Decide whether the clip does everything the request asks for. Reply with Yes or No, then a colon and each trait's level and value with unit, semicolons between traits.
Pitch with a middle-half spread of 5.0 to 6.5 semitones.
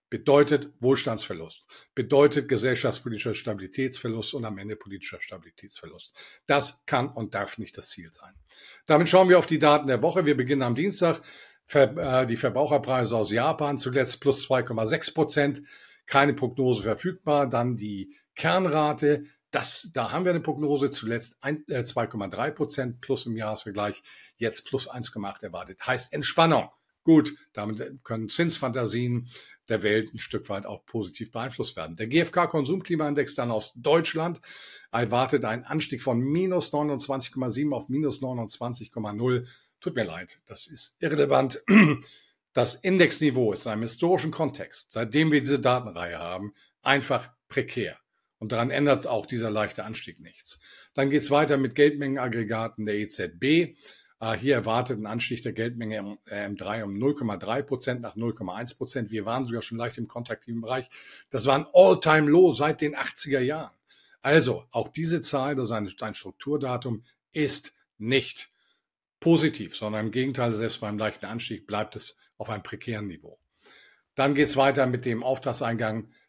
No: average, 4.5 semitones